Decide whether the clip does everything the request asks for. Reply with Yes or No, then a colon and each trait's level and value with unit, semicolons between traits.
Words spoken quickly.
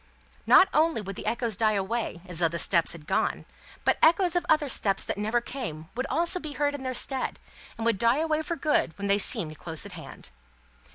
Yes: fast, 215 wpm